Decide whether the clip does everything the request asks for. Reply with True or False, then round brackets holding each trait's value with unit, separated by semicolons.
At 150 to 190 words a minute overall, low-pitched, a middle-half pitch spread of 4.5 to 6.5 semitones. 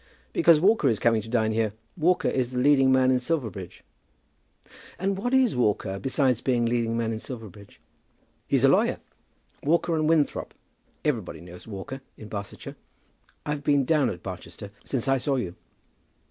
True (160 wpm; 125 Hz; 5.1 semitones)